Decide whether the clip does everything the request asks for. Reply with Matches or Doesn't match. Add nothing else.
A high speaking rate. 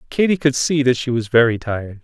Matches